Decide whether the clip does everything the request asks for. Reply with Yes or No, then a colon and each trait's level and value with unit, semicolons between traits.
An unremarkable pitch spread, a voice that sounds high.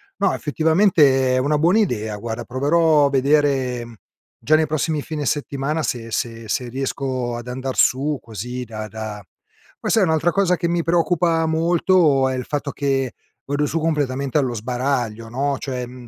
No: average, 4.2 semitones; medium, 140 Hz